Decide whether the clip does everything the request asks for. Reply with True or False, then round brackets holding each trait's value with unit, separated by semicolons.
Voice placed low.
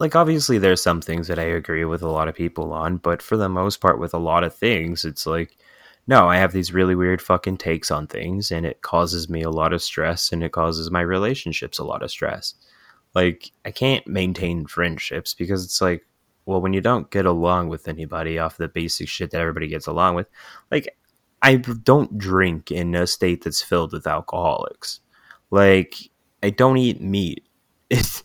True (90 Hz)